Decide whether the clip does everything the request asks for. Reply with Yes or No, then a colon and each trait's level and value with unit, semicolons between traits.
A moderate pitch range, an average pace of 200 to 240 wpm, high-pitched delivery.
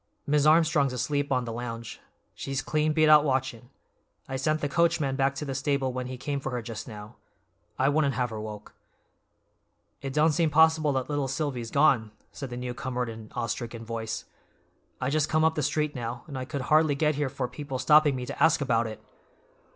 No: average, 3.6 semitones; fast, 205 wpm; low, 135 Hz